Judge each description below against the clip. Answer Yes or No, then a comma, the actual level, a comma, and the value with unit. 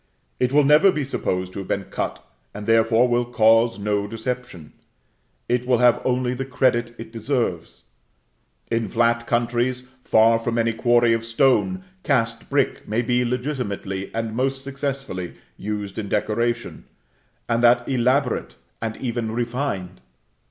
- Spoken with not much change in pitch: Yes, narrow, 2.1 semitones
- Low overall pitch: Yes, low, 120 Hz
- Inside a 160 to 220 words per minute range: No, average, 145 wpm